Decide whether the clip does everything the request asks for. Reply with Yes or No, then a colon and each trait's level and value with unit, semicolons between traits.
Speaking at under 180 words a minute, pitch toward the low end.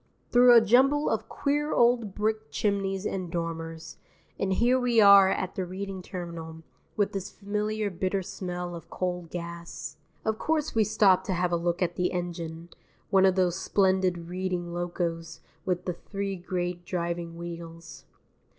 No: average, 160 wpm; medium, 185 Hz